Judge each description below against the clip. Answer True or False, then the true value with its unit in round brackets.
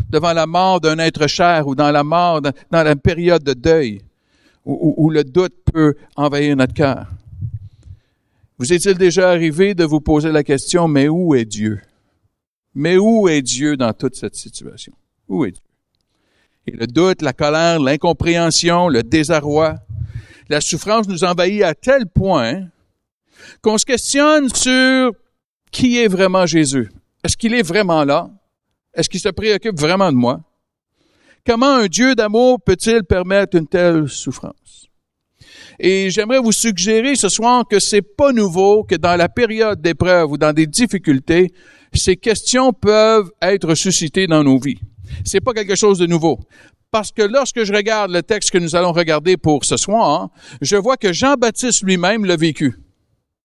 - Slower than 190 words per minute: True (165 wpm)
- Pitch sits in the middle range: True (175 Hz)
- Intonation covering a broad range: True (6.1 semitones)